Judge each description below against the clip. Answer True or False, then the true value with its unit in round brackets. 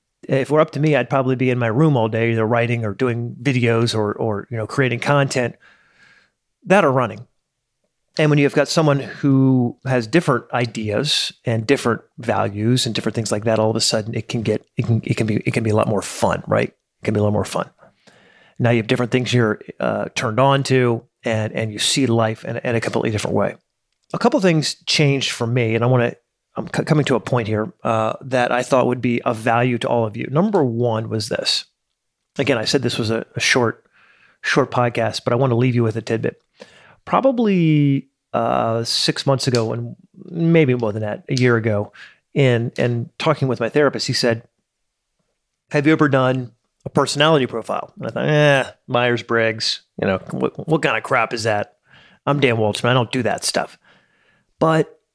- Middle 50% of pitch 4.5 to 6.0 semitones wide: False (3.5 semitones)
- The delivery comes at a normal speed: False (215 wpm)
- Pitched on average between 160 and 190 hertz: False (125 Hz)